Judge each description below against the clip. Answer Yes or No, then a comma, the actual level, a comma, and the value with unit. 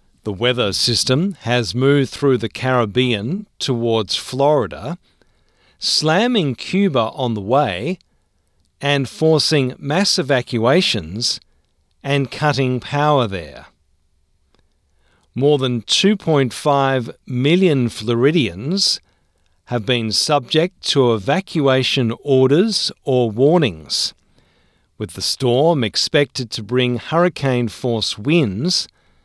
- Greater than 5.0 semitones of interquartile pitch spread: Yes, wide, 5.4 semitones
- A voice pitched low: Yes, low, 125 Hz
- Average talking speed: No, slow, 90 wpm